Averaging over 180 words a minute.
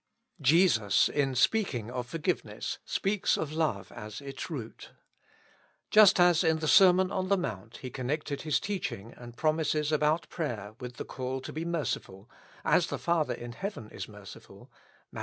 No: average, 160 wpm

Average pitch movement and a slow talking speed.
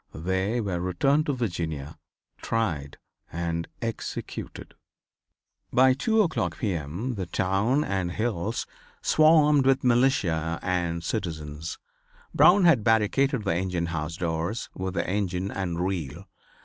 No: wide, 6.2 semitones; slow, 125 wpm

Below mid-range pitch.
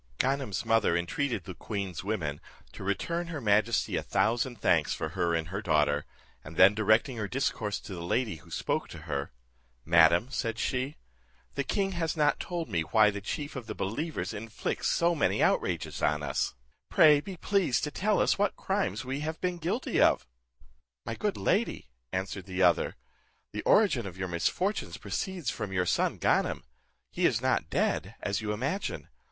Yes: low, 110 Hz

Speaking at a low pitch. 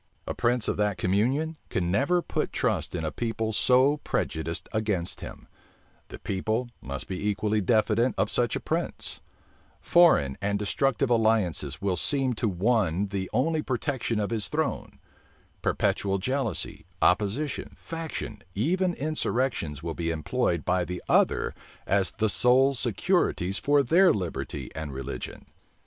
Yes: low, 110 Hz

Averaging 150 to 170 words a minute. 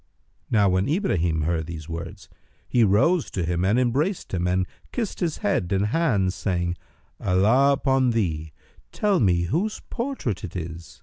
Yes: average, 160 wpm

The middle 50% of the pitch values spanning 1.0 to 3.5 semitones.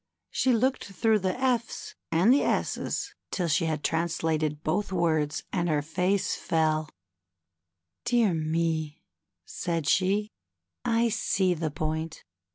No: average, 4.8 semitones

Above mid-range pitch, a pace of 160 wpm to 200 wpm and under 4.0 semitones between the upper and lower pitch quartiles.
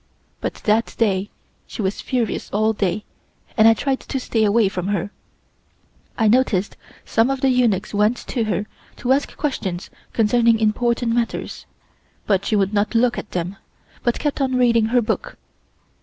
Yes: high, 225 Hz; average, 165 wpm; average, 3.0 semitones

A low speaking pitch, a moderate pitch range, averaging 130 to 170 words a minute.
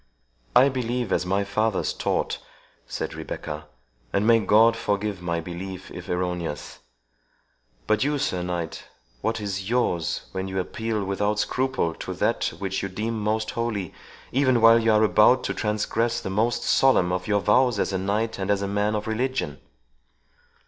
Yes: low, 105 Hz; average, 3.4 semitones; average, 165 wpm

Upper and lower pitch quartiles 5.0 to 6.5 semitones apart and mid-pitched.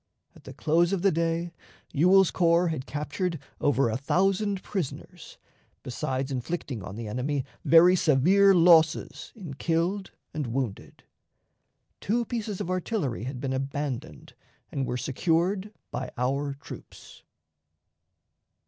Yes: wide, 5.4 semitones; medium, 160 Hz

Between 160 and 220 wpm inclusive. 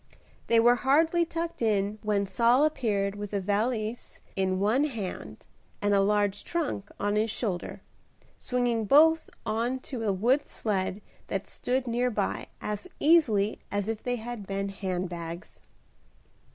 No: average, 150 wpm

